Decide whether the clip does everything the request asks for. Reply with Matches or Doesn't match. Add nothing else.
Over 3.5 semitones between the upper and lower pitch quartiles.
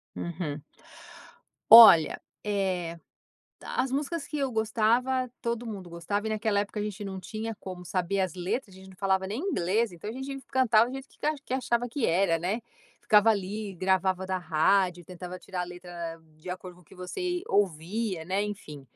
Matches